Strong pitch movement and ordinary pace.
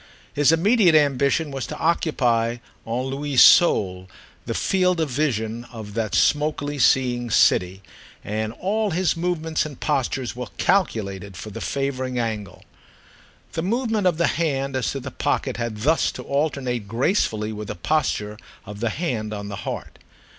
Yes: wide, 6.2 semitones; average, 155 wpm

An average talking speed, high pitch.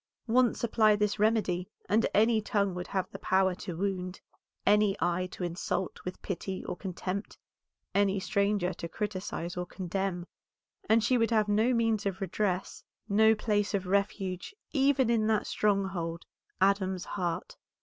Yes: average, 150 wpm; high, 200 Hz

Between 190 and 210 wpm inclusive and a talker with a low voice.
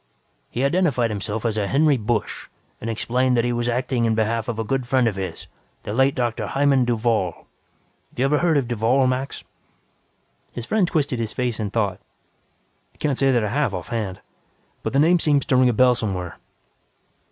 Yes: average, 195 wpm; low, 120 Hz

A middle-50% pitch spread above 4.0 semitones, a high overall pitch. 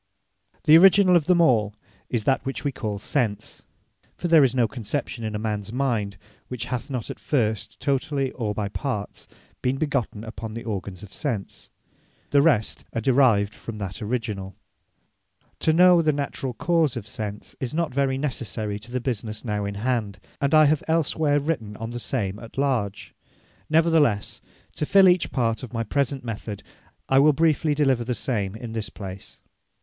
No: average, 5.2 semitones; low, 125 Hz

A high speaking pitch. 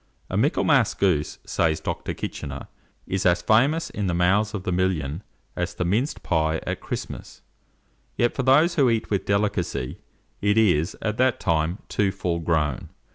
No: very low, 95 Hz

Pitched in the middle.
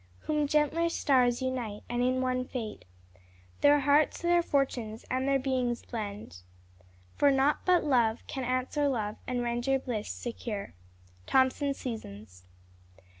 No: very high, 255 Hz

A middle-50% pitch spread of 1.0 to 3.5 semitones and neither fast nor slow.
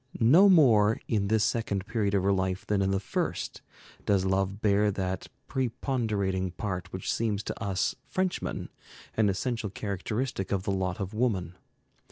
Yes: average, 2.9 semitones; average, 160 wpm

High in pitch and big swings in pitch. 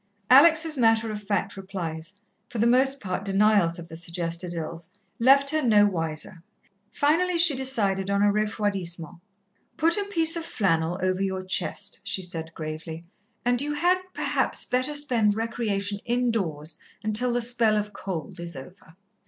Yes: high, 205 Hz; wide, 6.2 semitones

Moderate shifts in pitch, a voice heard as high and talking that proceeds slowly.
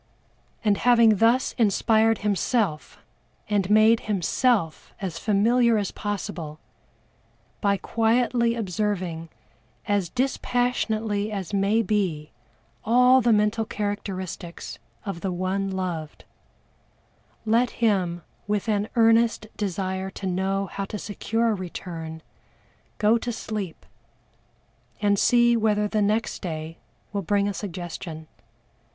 Yes: average, 3.2 semitones; high, 205 Hz; slow, 110 wpm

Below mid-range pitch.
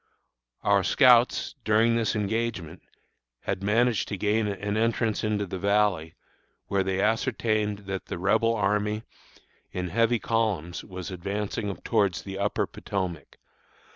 Yes: low, 105 Hz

